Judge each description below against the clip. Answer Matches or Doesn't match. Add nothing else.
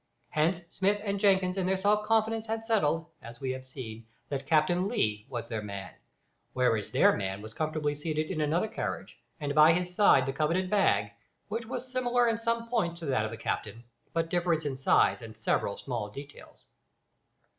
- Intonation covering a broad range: Matches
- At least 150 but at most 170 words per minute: Doesn't match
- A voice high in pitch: Doesn't match